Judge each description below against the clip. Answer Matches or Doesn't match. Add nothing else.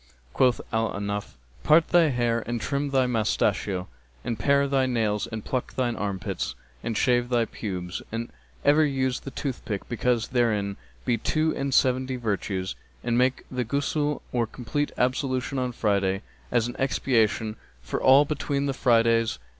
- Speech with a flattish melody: Doesn't match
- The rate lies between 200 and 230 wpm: Doesn't match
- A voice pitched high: Doesn't match